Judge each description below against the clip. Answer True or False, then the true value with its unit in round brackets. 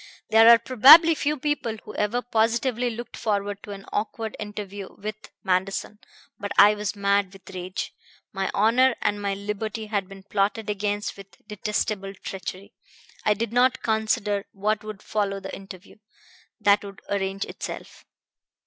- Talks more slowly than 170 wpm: True (150 wpm)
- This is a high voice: True (210 Hz)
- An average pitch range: False (2.0 semitones)